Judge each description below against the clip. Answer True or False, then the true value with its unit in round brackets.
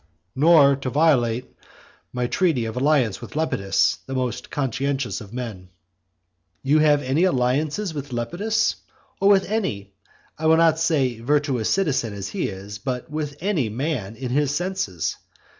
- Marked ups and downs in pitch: False (4.8 semitones)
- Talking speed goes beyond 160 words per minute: False (150 wpm)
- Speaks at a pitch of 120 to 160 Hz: True (135 Hz)